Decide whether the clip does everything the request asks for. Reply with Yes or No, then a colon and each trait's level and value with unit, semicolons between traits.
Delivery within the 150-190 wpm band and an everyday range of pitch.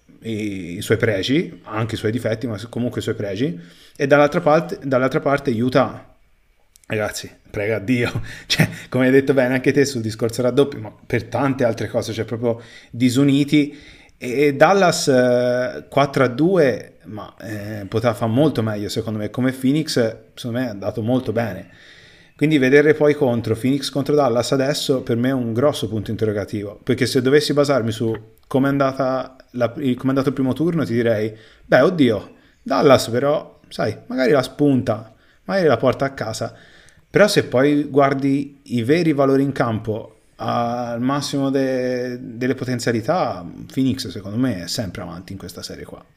Yes: average, 160 wpm; average, 3.8 semitones